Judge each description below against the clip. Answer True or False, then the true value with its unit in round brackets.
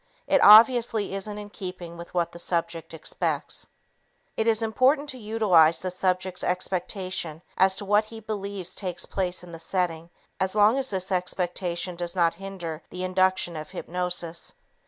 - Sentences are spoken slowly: False (160 wpm)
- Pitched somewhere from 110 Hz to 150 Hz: False (185 Hz)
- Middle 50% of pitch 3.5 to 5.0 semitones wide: False (3.1 semitones)